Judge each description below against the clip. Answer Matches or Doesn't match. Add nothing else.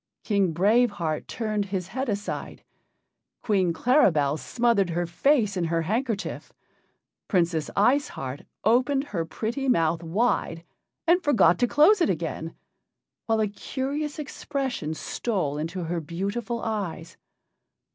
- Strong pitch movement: Matches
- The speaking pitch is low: Doesn't match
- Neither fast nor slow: Doesn't match